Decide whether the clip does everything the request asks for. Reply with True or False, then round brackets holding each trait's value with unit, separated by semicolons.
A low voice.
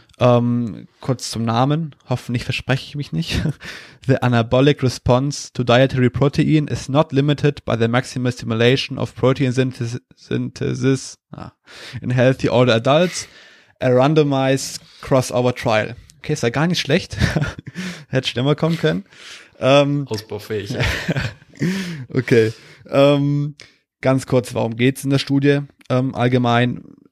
True (130 Hz)